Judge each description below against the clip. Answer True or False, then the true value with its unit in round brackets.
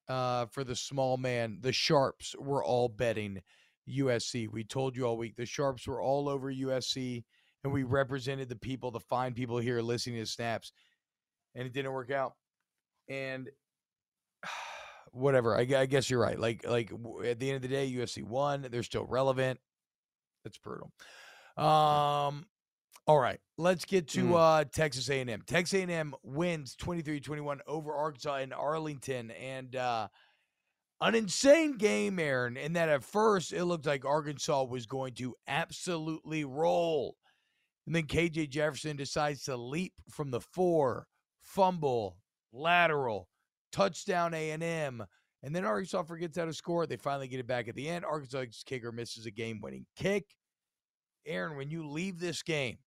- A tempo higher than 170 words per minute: False (155 wpm)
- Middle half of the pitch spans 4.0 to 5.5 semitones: True (4.3 semitones)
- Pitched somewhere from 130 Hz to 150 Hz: True (140 Hz)